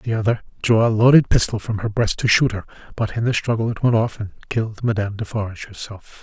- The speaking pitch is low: Yes, low, 110 Hz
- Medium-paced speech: No, fast, 230 wpm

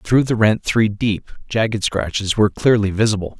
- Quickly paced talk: No, average, 175 wpm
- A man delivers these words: Yes, male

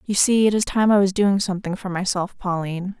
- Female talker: Yes, female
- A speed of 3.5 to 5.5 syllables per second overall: No, 5.9 syllables/s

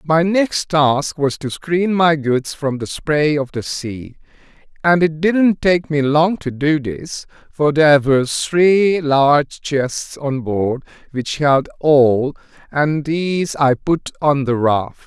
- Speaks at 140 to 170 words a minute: Yes, average, 165 wpm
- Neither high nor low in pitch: Yes, medium, 150 Hz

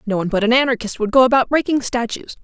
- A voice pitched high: Yes, high, 240 Hz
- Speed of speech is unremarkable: No, fast, 245 wpm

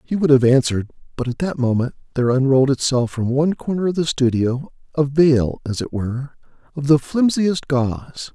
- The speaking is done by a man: Yes, male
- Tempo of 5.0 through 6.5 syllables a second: Yes, 5.5 syllables/s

